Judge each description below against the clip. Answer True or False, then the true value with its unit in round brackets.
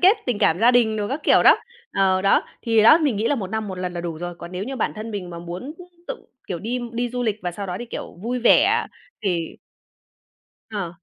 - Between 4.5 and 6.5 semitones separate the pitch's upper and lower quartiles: True (5.1 semitones)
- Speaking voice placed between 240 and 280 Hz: False (215 Hz)